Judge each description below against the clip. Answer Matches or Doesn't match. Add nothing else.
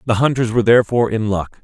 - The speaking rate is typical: Doesn't match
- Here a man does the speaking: Matches